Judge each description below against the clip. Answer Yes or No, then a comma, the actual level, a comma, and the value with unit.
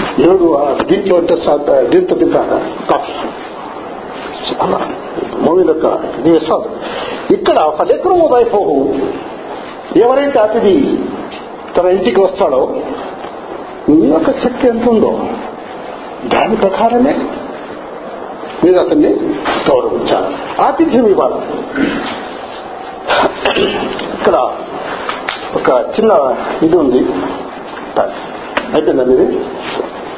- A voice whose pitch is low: No, very high, 275 Hz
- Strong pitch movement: Yes, wide, 8.8 semitones